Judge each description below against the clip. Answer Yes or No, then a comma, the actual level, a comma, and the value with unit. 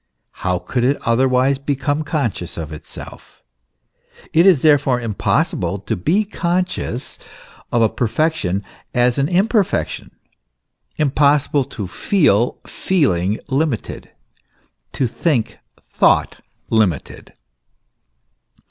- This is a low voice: Yes, low, 130 Hz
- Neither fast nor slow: No, slow, 95 wpm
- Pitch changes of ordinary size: No, wide, 5.7 semitones